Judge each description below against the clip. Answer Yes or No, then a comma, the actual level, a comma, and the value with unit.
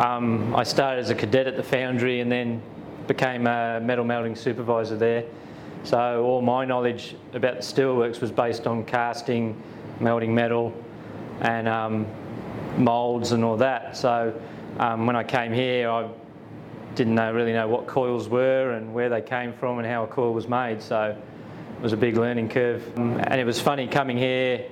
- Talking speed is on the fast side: No, average, 180 wpm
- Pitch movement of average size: No, narrow, 1.6 semitones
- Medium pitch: No, low, 120 Hz